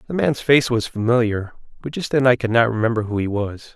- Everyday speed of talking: No, fast, 240 wpm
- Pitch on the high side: No, low, 115 Hz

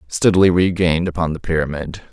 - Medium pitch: No, very low, 85 Hz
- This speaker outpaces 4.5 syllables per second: Yes, 6.4 syllables/s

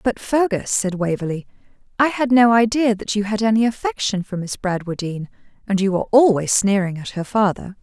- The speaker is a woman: Yes, female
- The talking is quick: No, average, 185 wpm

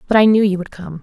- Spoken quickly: Yes, fast, 350 wpm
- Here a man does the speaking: No, female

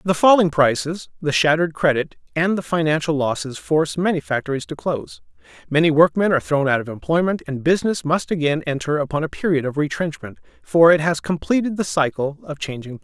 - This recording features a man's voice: Yes, male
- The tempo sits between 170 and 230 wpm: Yes, average, 190 wpm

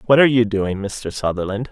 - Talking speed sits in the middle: No, fast, 210 wpm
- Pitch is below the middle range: Yes, low, 110 Hz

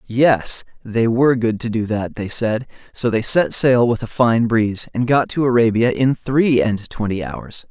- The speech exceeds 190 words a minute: Yes, average, 200 wpm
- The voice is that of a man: Yes, male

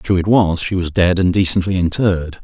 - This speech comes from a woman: No, male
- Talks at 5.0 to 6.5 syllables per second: Yes, 5.5 syllables/s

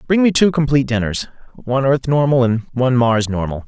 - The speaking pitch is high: No, low, 130 Hz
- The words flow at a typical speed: Yes, average, 180 wpm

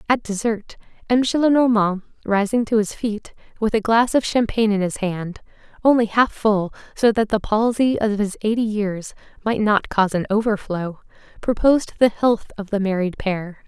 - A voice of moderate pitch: No, high, 215 Hz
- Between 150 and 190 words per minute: Yes, average, 160 wpm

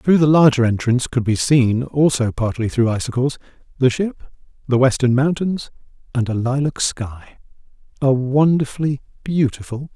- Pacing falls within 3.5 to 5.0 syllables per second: No, 5.2 syllables/s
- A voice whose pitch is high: No, low, 130 Hz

